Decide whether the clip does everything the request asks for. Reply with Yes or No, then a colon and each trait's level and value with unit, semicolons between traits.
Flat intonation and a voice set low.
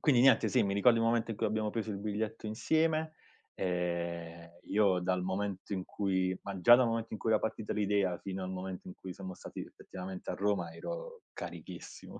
No: average, 3.5 semitones; low, 100 Hz